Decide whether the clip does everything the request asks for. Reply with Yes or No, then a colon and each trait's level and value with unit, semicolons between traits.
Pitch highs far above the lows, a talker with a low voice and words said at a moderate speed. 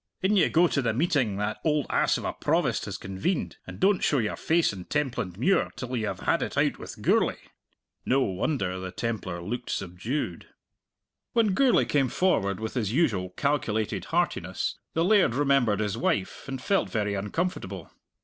Yes: wide, 7.5 semitones; low, 120 Hz; average, 175 wpm